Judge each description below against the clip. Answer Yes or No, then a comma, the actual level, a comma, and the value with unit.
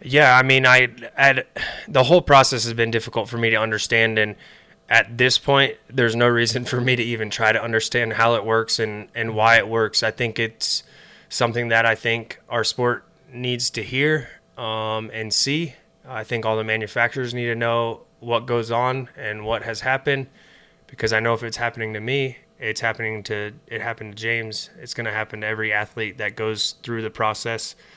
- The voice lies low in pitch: Yes, low, 115 Hz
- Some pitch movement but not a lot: No, narrow, 2.3 semitones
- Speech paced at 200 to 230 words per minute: Yes, fast, 205 wpm